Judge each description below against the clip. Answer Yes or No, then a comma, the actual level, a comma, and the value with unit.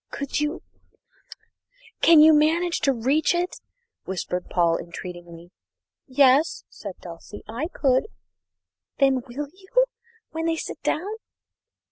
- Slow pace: Yes, slow, 115 wpm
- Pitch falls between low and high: No, very high, 280 Hz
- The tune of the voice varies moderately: No, wide, 8.6 semitones